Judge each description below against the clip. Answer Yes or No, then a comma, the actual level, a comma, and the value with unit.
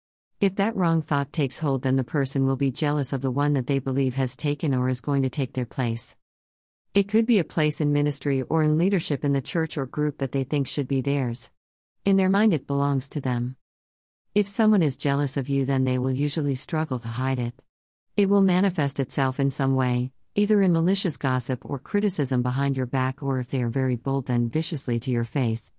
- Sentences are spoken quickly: Yes, fast, 225 wpm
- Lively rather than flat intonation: No, average, 3.1 semitones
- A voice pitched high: No, low, 135 Hz